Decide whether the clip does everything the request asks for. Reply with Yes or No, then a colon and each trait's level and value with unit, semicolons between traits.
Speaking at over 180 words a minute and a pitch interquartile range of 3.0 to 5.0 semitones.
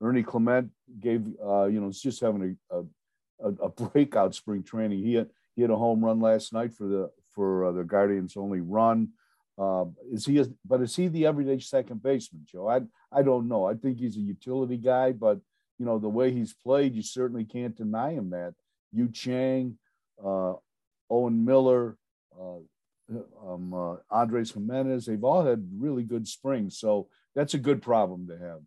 Yes: average, 190 wpm; average, 4.4 semitones